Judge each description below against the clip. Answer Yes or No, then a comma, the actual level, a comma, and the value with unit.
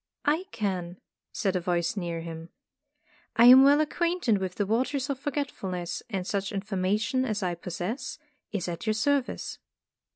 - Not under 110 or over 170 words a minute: Yes, average, 160 wpm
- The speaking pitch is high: Yes, high, 205 Hz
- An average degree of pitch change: No, wide, 6.4 semitones